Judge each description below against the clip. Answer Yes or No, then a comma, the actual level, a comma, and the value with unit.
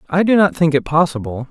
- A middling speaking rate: No, fast, 240 wpm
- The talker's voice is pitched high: No, medium, 160 Hz